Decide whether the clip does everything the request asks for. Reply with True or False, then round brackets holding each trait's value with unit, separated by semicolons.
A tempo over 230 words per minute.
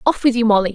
True (325 wpm)